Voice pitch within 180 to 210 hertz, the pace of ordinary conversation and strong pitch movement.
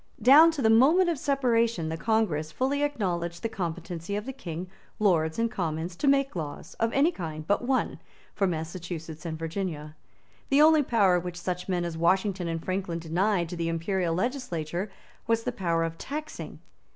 Yes: medium, 185 Hz; average, 175 wpm; wide, 5.8 semitones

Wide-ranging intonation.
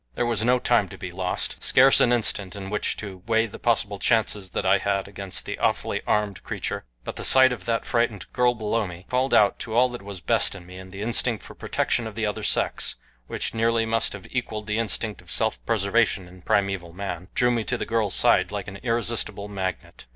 No: average, 3.0 semitones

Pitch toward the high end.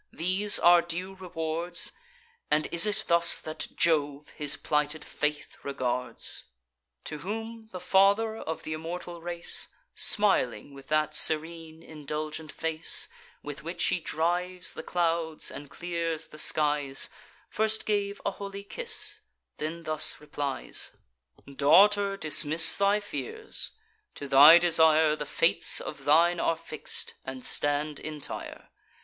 No: medium, 165 Hz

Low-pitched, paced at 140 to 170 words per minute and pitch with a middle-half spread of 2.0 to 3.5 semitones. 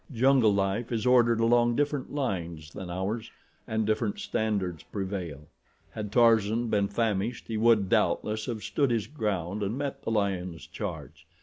Yes: low, 110 Hz; average, 150 wpm; average, 3.2 semitones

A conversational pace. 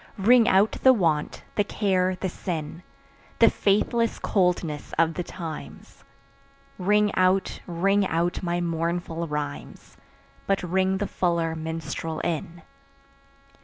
No: slow, 120 wpm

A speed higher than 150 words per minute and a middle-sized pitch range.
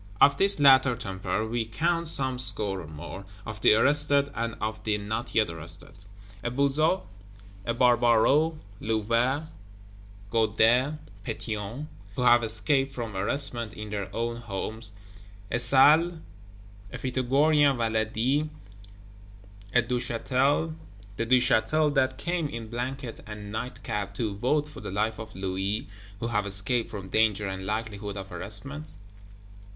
No: slow, 135 wpm; average, 4.2 semitones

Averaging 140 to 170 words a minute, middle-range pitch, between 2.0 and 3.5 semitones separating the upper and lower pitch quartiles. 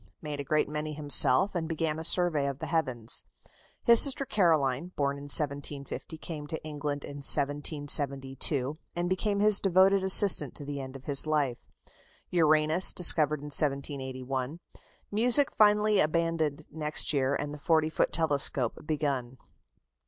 Yes: average, 145 wpm; medium, 150 Hz; average, 3.0 semitones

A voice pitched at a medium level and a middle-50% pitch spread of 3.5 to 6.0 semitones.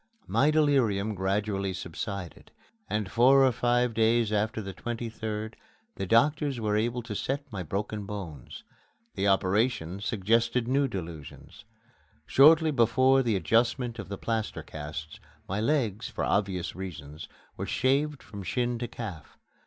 No: low, 110 Hz; average, 4.0 semitones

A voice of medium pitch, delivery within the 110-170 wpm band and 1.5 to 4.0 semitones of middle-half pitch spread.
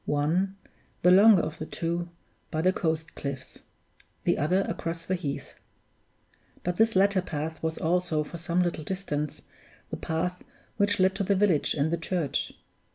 Yes: medium, 170 Hz; average, 160 wpm; average, 3.0 semitones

